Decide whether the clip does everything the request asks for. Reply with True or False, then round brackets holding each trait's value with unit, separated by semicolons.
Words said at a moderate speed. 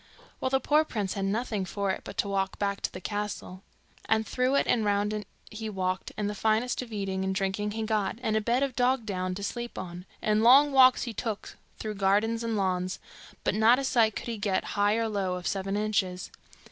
False (225 wpm)